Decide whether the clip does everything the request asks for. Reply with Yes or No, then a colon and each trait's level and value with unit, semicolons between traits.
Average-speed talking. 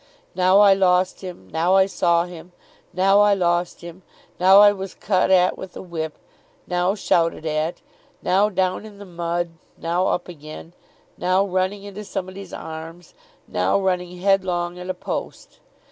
Yes: average, 160 wpm